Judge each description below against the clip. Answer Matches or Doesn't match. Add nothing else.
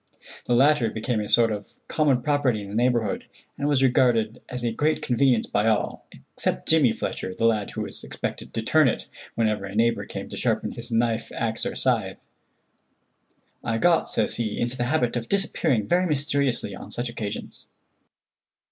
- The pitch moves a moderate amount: Matches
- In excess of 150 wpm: Matches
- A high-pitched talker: Doesn't match